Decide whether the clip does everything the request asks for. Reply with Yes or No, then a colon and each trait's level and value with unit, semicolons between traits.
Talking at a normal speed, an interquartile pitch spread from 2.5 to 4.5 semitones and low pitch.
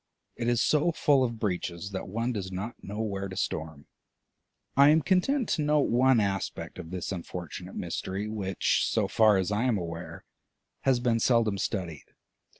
No: average, 170 wpm; average, 4.9 semitones; low, 105 Hz